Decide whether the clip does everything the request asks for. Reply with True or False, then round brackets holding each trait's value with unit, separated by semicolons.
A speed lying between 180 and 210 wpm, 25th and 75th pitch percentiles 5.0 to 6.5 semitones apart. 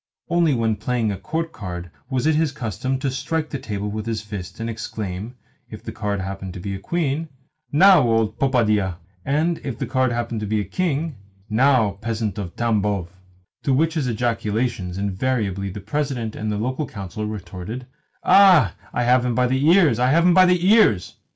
True (195 wpm; 5.3 semitones)